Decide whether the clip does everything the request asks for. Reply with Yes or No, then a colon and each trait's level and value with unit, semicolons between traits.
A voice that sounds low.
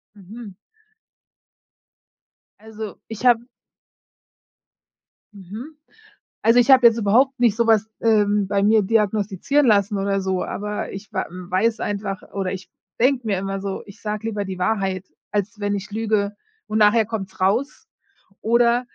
No: high, 210 Hz